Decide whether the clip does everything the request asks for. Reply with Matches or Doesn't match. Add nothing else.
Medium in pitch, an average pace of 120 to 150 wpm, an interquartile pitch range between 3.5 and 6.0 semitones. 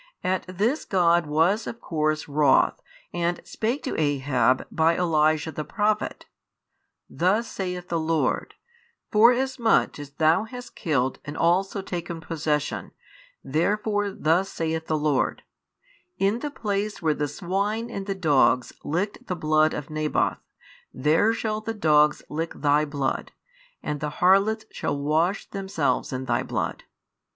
Matches